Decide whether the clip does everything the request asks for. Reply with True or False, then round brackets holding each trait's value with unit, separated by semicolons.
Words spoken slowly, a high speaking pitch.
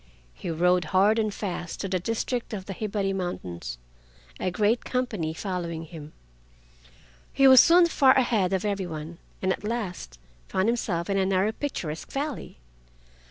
False (160 wpm; 195 Hz)